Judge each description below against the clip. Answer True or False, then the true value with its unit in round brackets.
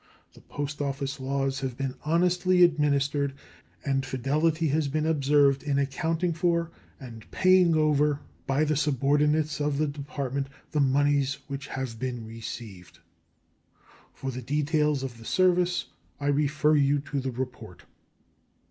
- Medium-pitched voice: True (145 Hz)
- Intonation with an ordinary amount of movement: False (2.3 semitones)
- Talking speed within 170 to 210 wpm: False (140 wpm)